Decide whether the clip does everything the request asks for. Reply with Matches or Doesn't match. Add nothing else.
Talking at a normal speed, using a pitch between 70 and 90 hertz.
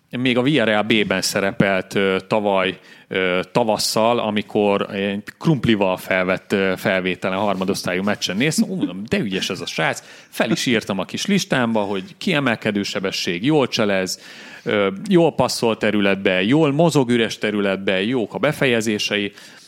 Doesn't match